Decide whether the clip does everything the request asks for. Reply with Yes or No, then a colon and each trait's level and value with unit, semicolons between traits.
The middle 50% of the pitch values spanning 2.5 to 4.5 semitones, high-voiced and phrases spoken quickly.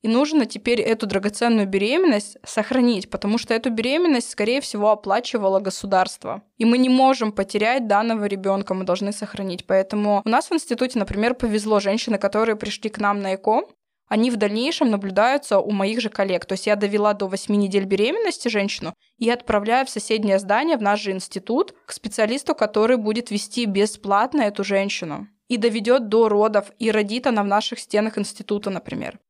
Yes: average, 2.9 semitones; high, 215 Hz; fast, 175 wpm